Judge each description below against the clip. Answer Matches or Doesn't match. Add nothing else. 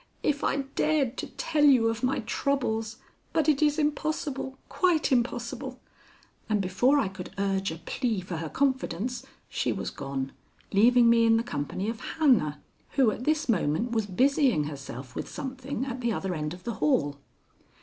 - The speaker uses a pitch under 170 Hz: Doesn't match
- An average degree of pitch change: Doesn't match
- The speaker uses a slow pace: Doesn't match